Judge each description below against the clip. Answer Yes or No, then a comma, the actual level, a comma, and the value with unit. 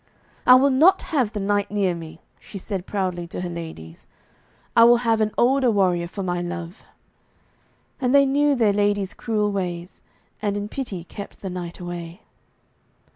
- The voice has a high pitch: Yes, high, 200 Hz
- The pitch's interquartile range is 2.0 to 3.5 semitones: No, average, 4.6 semitones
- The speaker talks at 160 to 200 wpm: Yes, average, 170 wpm